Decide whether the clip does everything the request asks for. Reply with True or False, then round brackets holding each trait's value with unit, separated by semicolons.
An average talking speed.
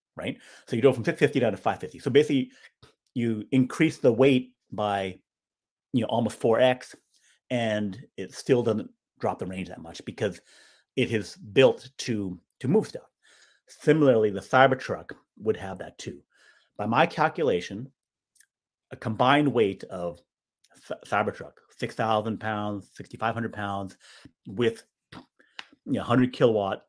True (155 wpm)